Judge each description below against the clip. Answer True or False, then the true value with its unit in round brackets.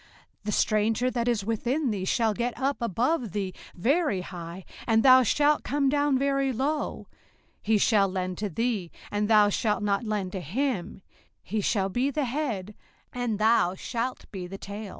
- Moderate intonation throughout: True (4.7 semitones)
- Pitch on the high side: True (220 Hz)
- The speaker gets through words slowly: False (180 wpm)